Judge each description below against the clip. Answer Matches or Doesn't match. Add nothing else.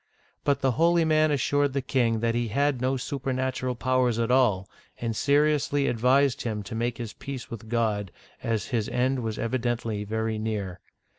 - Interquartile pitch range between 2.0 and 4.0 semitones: Matches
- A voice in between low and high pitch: Doesn't match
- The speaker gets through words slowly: Doesn't match